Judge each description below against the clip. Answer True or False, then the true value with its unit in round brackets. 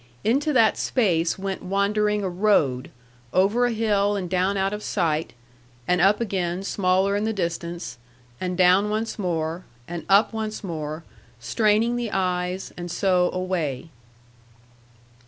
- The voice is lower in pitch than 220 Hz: True (190 Hz)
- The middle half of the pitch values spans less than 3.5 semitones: True (3.1 semitones)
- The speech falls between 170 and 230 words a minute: False (140 wpm)